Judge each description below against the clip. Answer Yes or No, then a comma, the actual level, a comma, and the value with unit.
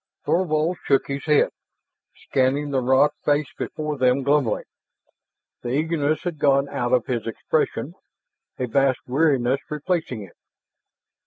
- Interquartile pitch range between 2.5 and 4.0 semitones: Yes, average, 3.0 semitones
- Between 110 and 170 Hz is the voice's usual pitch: Yes, medium, 140 Hz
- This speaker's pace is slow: Yes, slow, 130 wpm